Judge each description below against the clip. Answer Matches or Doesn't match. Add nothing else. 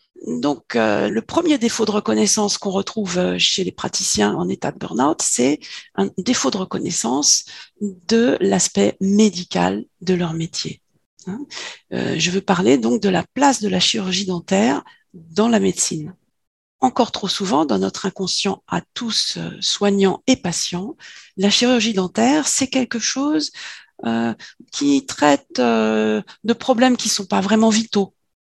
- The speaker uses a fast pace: Doesn't match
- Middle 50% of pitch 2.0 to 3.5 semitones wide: Doesn't match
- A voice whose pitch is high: Matches